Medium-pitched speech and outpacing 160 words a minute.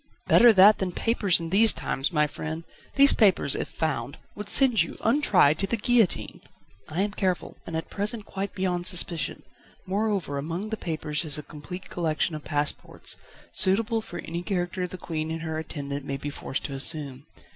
Yes: medium, 175 Hz; average, 180 wpm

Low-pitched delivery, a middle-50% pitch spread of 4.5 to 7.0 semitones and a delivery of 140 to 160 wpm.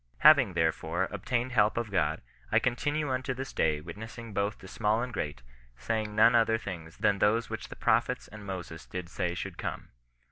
No: low, 105 Hz; average, 5.0 semitones; average, 185 wpm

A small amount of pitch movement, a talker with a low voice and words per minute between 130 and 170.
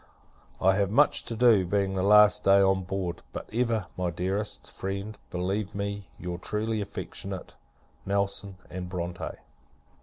Yes: narrow, 2.1 semitones; low, 100 Hz; average, 145 wpm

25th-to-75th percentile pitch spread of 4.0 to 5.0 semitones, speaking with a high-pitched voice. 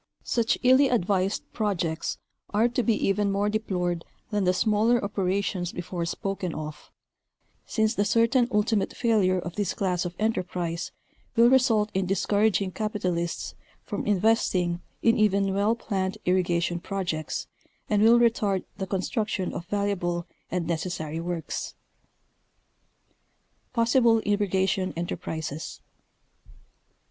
No: average, 3.5 semitones; high, 195 Hz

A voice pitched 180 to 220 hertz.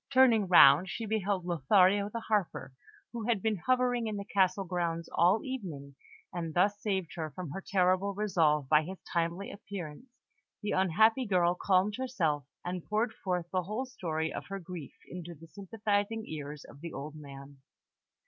Yes: medium, 185 Hz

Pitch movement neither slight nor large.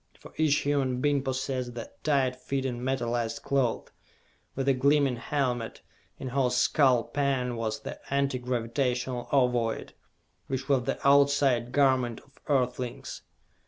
No: narrow, 2.2 semitones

